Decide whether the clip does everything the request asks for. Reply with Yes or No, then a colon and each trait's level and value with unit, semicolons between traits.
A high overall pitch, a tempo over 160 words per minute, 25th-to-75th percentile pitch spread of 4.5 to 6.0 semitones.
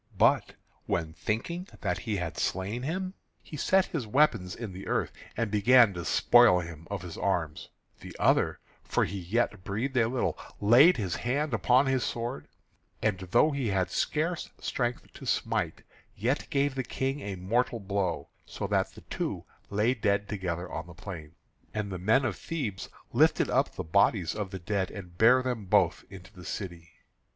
No: low, 105 Hz; average, 180 wpm; wide, 5.4 semitones